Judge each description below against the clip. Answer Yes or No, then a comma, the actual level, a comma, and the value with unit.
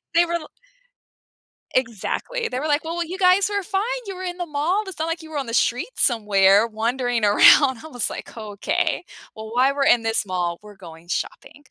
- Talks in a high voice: Yes, very high, 260 Hz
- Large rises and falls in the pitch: Yes, wide, 7.8 semitones